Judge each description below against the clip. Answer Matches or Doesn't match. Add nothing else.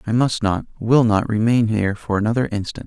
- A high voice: Doesn't match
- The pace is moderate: Matches